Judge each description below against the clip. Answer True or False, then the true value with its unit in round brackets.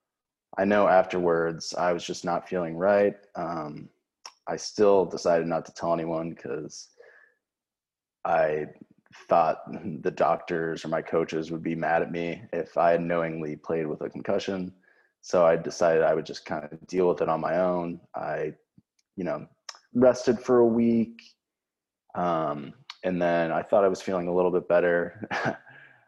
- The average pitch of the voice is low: True (85 Hz)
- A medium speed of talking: True (165 wpm)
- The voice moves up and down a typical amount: False (2.1 semitones)